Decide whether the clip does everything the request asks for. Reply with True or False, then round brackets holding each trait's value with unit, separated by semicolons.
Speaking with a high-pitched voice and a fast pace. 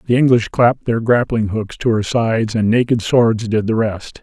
False (115 Hz; 215 wpm)